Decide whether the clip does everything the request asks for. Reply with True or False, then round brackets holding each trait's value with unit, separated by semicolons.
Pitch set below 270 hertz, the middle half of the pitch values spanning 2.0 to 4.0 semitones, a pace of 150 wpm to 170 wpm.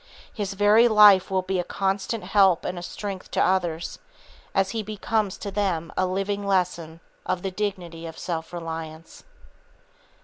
True (190 Hz; 2.8 semitones; 160 wpm)